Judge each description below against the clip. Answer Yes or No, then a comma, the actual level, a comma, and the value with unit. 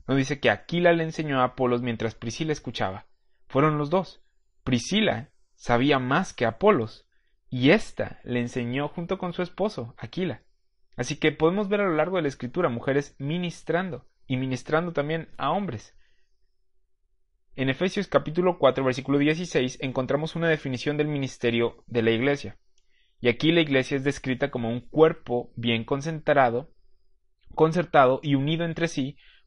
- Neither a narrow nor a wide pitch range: Yes, average, 4.6 semitones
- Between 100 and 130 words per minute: No, average, 155 wpm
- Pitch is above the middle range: No, medium, 140 Hz